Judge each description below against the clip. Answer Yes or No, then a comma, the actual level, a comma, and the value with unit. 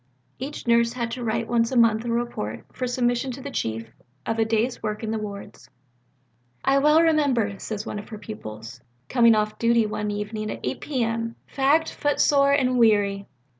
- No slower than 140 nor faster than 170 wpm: No, average, 185 wpm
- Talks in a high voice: Yes, high, 230 Hz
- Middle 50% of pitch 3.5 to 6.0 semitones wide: No, average, 3.1 semitones